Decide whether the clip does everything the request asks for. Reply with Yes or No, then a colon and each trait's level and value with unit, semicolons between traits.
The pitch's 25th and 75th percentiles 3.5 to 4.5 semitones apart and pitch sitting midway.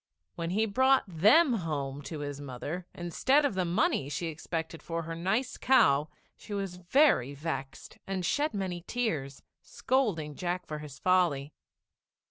No: average, 5.3 semitones; medium, 175 Hz